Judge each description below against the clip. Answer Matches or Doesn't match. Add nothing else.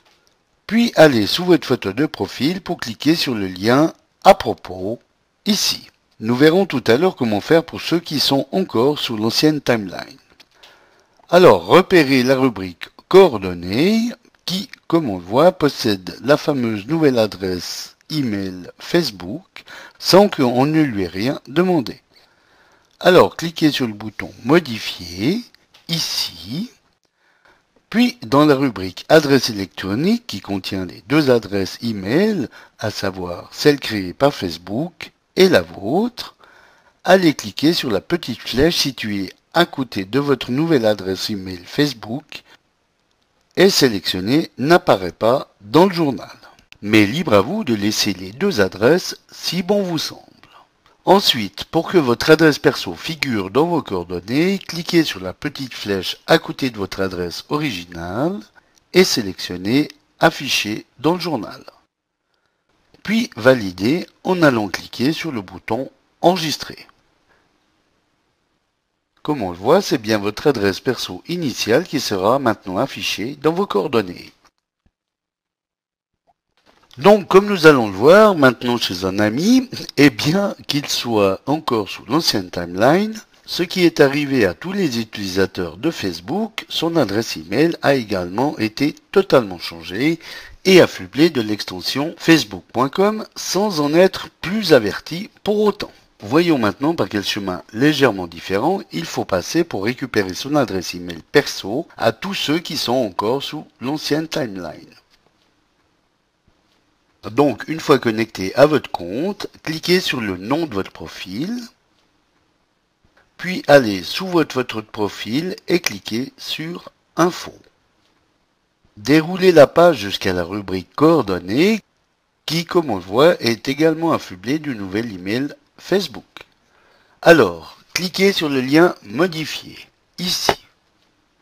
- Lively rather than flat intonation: Matches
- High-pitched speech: Doesn't match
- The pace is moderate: Doesn't match